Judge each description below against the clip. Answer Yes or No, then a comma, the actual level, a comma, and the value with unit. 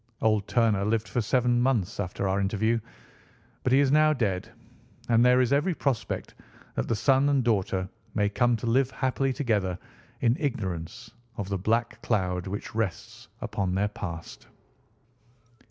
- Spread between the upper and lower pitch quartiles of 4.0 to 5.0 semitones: Yes, average, 4.3 semitones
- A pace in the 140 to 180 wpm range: Yes, average, 155 wpm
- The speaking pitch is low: Yes, low, 115 Hz